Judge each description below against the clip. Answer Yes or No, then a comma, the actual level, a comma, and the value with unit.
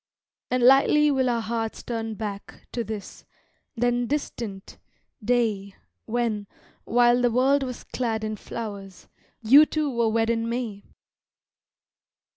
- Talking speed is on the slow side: Yes, slow, 125 wpm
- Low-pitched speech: No, high, 235 Hz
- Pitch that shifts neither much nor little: No, narrow, 2.2 semitones